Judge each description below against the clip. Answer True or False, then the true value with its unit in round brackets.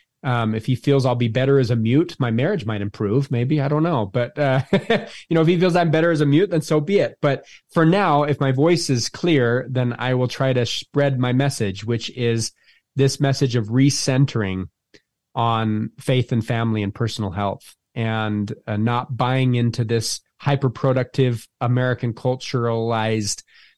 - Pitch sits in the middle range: False (125 Hz)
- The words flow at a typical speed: True (180 wpm)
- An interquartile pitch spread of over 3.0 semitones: True (3.4 semitones)